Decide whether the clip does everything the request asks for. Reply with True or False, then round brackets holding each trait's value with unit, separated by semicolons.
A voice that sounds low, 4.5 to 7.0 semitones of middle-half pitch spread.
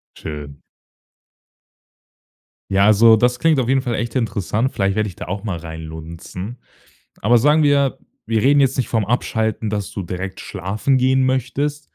True (110 Hz; 5.2 semitones)